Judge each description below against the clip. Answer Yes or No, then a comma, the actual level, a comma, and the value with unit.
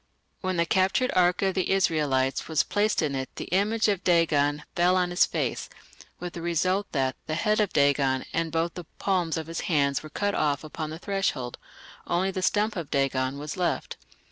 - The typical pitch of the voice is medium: Yes, medium, 170 Hz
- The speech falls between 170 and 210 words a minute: Yes, average, 195 wpm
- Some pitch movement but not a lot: Yes, average, 4.3 semitones